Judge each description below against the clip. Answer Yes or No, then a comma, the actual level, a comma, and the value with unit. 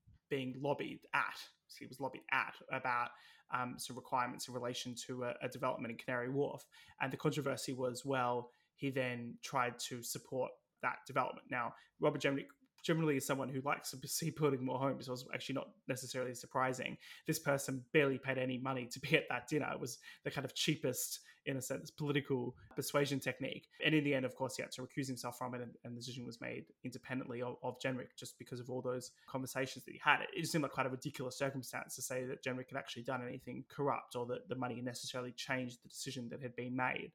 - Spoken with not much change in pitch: Yes, narrow, 1.9 semitones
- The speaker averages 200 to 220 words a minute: Yes, fast, 215 wpm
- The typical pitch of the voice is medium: No, low, 130 Hz